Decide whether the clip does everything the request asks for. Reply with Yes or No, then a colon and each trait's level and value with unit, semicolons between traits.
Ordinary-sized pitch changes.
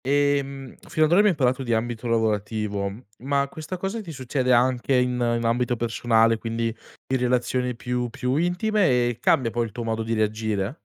Yes: average, 3.2 semitones